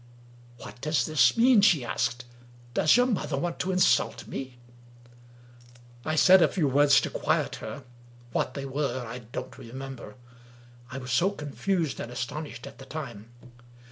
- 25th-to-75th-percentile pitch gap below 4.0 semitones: No, average, 4.7 semitones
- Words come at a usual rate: Yes, average, 165 wpm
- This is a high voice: No, medium, 140 Hz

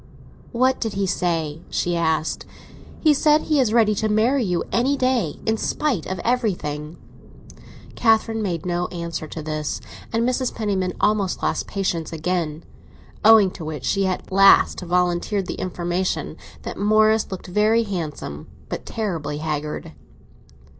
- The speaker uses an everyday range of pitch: Yes, average, 5.0 semitones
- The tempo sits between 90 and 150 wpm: Yes, average, 145 wpm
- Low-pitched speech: No, high, 190 Hz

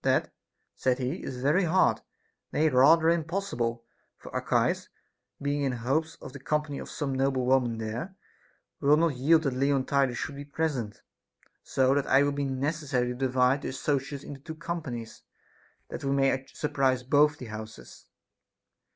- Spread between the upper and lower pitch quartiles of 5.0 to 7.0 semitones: No, average, 2.9 semitones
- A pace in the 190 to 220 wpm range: No, average, 165 wpm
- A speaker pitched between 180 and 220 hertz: No, low, 135 Hz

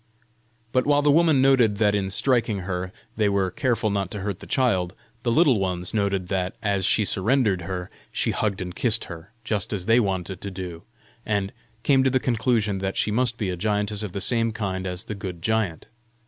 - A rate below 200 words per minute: No, fast, 205 wpm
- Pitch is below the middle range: Yes, low, 100 Hz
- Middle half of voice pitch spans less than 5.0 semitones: Yes, average, 3.6 semitones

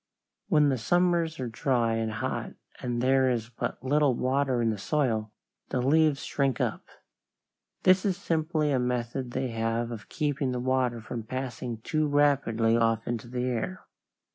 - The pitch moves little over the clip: No, average, 3.8 semitones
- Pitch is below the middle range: Yes, low, 130 Hz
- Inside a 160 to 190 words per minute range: Yes, average, 165 wpm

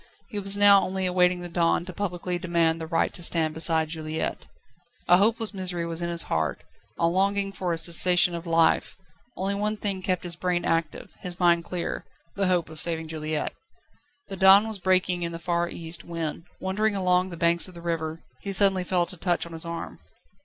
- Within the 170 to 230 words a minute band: Yes, fast, 205 wpm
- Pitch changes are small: Yes, narrow, 2.1 semitones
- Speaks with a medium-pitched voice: Yes, medium, 175 Hz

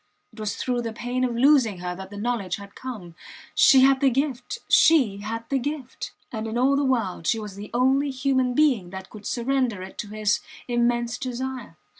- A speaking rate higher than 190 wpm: Yes, average, 200 wpm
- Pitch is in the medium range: No, high, 240 Hz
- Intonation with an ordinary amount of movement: Yes, average, 3.9 semitones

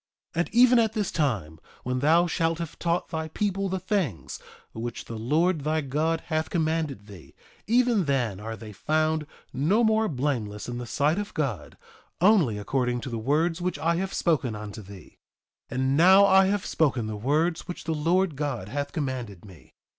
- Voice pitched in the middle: Yes, medium, 155 Hz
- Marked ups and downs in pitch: Yes, wide, 6.5 semitones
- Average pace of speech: Yes, average, 185 wpm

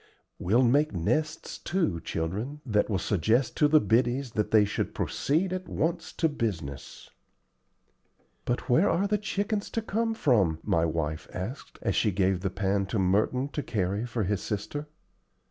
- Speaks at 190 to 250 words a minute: No, average, 165 wpm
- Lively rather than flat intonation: Yes, wide, 7.9 semitones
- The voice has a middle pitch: No, low, 115 Hz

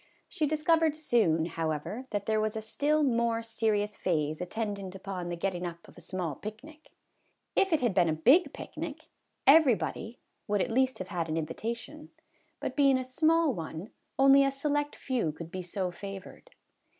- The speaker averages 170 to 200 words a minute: Yes, average, 175 wpm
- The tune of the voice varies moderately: No, wide, 7.4 semitones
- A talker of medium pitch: No, high, 220 Hz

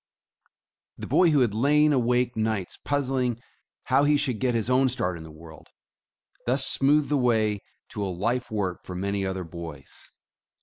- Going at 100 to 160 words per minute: No, average, 170 wpm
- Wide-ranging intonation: Yes, wide, 5.9 semitones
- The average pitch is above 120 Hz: No, low, 115 Hz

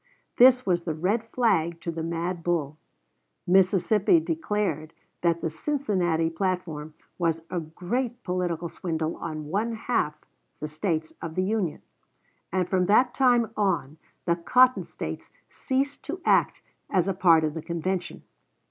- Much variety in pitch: No, average, 4.8 semitones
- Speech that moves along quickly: No, average, 145 wpm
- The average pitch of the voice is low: No, medium, 180 Hz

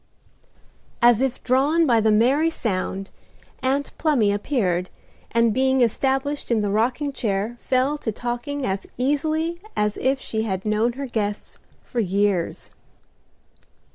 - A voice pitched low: No, high, 240 Hz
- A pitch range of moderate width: Yes, average, 4.5 semitones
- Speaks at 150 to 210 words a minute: No, slow, 135 wpm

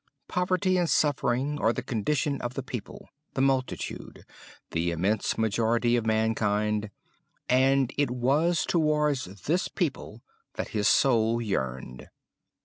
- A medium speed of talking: No, slow, 125 wpm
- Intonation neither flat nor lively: Yes, average, 5.0 semitones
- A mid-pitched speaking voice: No, low, 125 Hz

